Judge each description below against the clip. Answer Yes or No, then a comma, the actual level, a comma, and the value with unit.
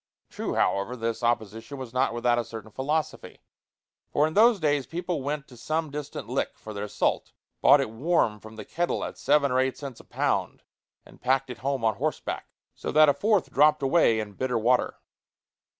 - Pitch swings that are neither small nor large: Yes, average, 4.7 semitones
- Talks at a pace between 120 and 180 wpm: No, average, 195 wpm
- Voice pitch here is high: No, low, 130 Hz